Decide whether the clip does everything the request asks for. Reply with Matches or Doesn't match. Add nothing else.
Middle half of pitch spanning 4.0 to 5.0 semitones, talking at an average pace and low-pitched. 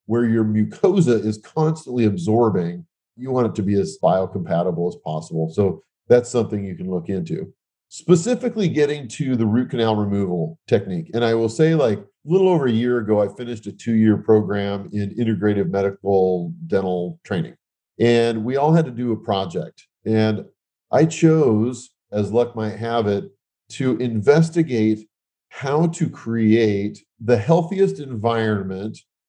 Matches